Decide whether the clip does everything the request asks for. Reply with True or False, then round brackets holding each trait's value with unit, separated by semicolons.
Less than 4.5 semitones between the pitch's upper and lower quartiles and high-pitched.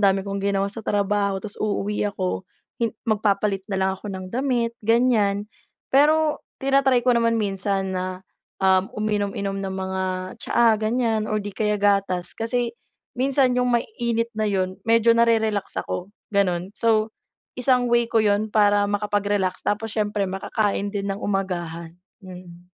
True (2.8 semitones; 205 Hz)